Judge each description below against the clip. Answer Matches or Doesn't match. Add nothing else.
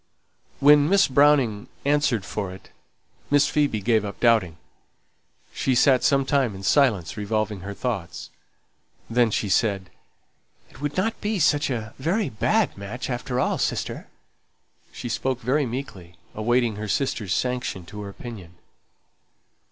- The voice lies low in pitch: Matches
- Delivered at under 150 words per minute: Matches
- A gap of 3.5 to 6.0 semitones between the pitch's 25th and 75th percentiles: Matches